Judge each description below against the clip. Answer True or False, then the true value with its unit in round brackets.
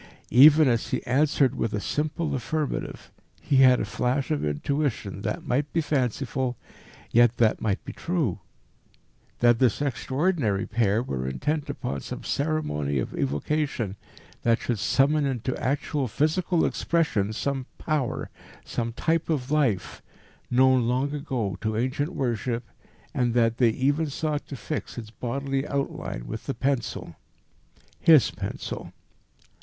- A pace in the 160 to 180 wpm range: False (140 wpm)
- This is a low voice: True (130 Hz)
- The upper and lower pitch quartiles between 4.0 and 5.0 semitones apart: True (4.3 semitones)